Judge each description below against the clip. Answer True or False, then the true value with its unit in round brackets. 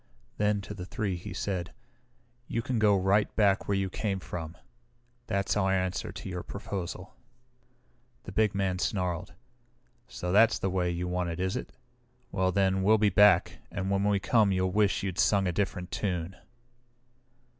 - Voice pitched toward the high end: False (95 Hz)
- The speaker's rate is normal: True (170 wpm)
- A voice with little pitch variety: True (2.0 semitones)